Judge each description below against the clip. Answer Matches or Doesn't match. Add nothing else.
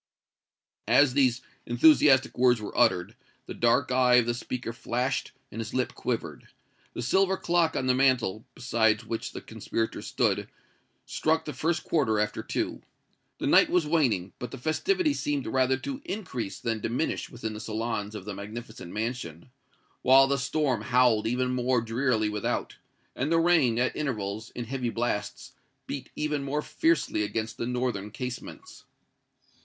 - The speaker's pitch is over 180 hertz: Doesn't match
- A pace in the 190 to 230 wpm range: Doesn't match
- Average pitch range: Matches